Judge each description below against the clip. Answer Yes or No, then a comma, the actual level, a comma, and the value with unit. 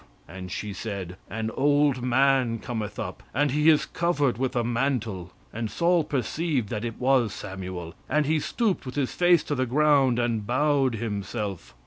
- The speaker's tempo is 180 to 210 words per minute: No, average, 170 wpm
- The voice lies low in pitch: Yes, low, 125 Hz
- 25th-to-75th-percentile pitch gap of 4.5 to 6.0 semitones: Yes, average, 5.1 semitones